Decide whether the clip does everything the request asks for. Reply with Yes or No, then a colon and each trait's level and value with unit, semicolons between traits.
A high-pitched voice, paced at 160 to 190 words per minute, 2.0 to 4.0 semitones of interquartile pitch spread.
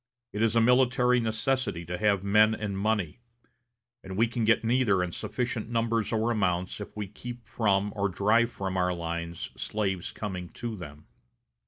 No: low, 105 Hz; average, 170 wpm; average, 3.6 semitones